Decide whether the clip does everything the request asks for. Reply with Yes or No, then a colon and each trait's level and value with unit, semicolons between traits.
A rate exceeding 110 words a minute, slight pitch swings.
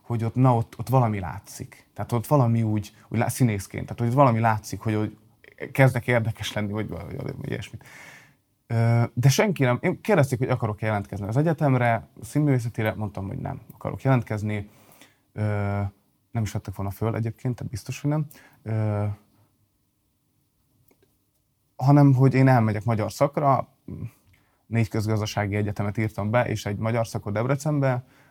No: average, 150 wpm; average, 4.0 semitones